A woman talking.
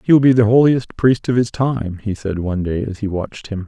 No: male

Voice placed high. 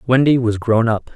No: low, 120 Hz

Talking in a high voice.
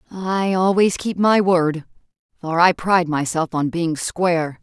No: medium, 175 Hz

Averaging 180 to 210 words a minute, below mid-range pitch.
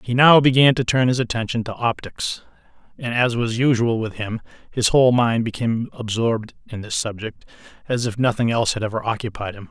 Yes: average, 190 wpm; low, 115 Hz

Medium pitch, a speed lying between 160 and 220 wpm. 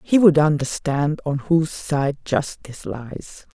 No: medium, 150 Hz; slow, 135 wpm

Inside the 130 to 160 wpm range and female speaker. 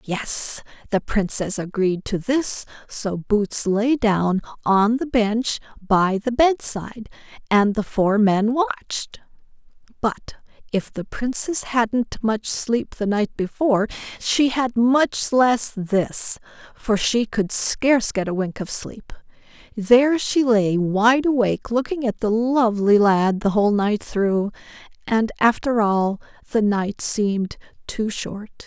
Yes: average, 140 wpm; female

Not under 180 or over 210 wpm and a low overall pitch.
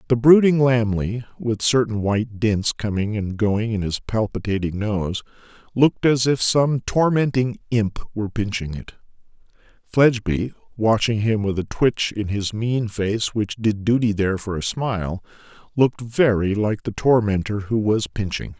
No: average, 155 wpm; low, 110 Hz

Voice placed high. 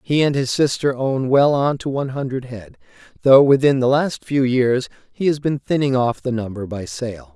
No: low, 130 Hz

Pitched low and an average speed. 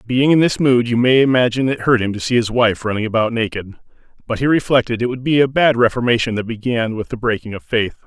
No: low, 120 Hz; fast, 230 wpm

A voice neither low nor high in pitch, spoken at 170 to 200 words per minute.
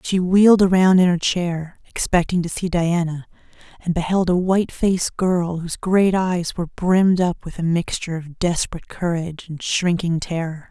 Yes: medium, 175 Hz; average, 175 wpm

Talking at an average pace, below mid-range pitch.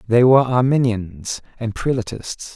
No: slow, 120 wpm; low, 115 Hz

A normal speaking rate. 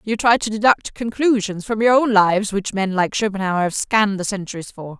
No: fast, 215 wpm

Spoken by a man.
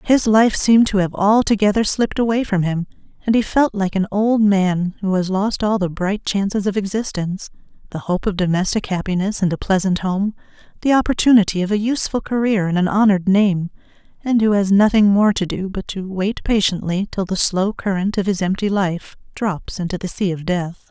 No: female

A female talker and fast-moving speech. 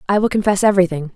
Yes: female; fast, 210 wpm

